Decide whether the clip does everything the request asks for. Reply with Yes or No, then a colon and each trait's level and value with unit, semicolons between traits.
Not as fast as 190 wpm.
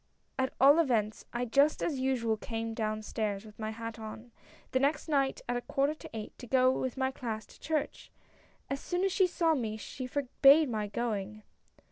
No: average, 195 wpm